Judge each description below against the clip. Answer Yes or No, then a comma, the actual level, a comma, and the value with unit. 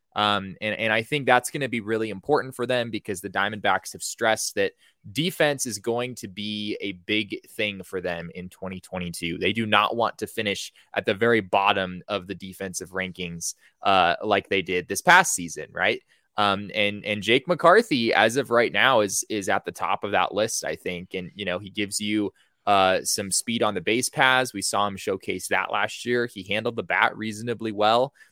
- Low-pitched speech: Yes, low, 105 Hz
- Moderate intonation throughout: Yes, average, 3.6 semitones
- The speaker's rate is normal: No, fast, 210 wpm